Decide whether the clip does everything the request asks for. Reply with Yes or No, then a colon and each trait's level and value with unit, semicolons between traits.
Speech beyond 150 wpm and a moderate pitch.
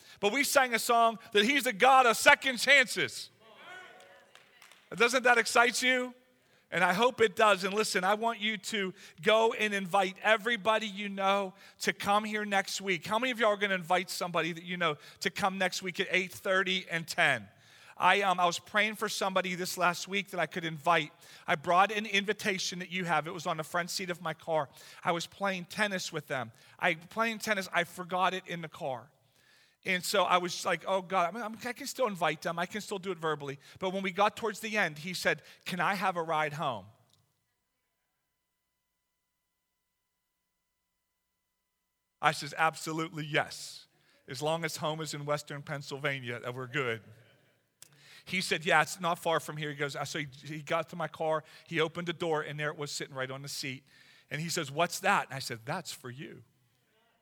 Yes: average, 200 wpm; medium, 180 Hz